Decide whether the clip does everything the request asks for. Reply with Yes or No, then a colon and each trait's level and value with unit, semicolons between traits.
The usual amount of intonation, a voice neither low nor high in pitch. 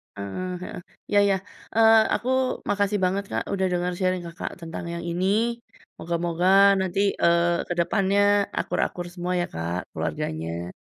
No: narrow, 2.3 semitones; medium, 175 Hz